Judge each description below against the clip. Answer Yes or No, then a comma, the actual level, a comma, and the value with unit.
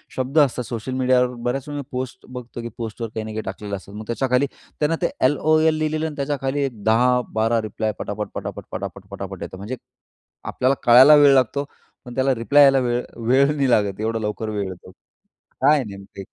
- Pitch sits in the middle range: No, low, 125 Hz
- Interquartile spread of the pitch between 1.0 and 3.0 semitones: No, average, 3.9 semitones